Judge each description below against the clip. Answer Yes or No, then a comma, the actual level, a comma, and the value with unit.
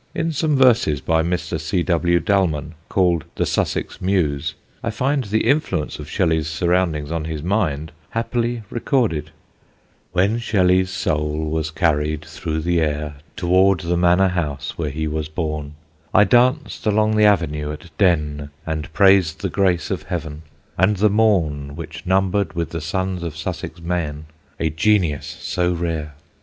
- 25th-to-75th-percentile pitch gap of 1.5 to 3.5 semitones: No, average, 3.9 semitones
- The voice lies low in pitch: Yes, very low, 85 Hz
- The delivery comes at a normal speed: Yes, average, 155 wpm